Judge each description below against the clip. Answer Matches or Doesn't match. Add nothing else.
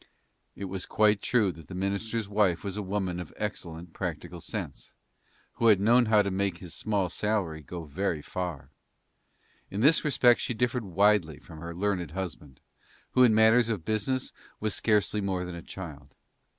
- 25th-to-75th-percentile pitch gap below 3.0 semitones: Doesn't match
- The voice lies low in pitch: Matches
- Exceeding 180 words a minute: Doesn't match